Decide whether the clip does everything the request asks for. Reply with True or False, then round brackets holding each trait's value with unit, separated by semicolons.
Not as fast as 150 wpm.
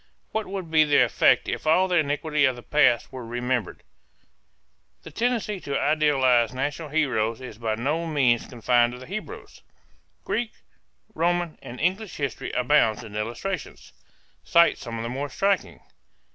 False (155 wpm)